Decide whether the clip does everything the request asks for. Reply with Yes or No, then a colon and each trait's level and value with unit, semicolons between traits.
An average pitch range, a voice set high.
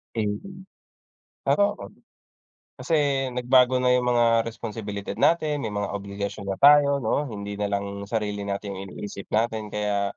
No: average, 3.7 semitones; low, 110 Hz